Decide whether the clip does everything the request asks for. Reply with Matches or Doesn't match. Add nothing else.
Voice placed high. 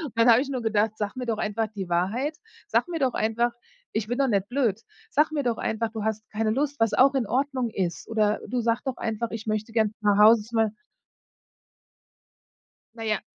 Matches